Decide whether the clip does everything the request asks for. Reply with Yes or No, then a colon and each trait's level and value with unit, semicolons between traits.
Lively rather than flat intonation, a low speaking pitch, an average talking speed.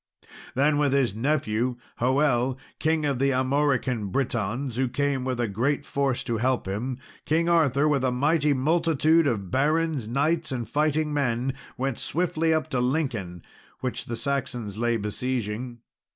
No: average, 3.6 semitones; low, 130 Hz; average, 150 wpm